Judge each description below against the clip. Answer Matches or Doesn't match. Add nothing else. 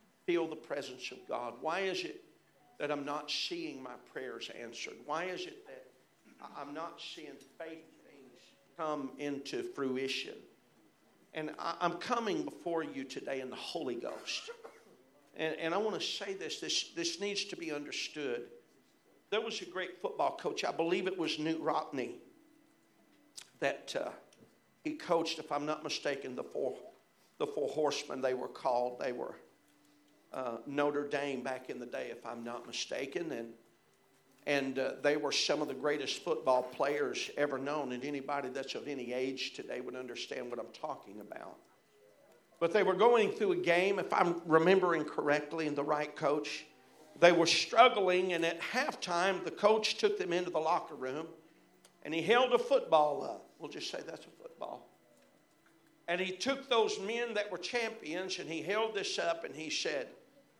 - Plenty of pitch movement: Matches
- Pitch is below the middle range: Doesn't match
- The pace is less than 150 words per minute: Doesn't match